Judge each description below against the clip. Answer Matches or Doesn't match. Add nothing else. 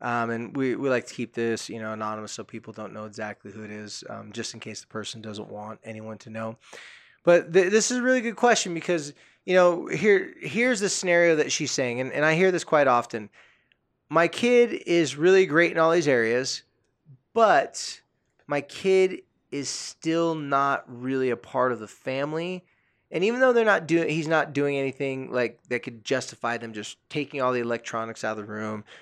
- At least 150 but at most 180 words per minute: Doesn't match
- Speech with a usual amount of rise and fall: Doesn't match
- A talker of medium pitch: Doesn't match